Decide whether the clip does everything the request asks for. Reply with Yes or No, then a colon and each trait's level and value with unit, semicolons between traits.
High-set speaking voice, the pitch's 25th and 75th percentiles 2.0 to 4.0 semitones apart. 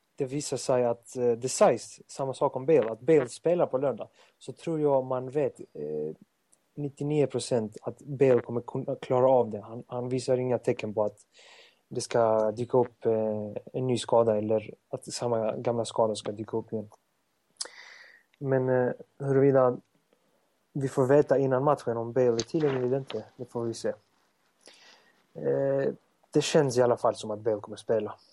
No: low, 125 Hz; average, 3.2 semitones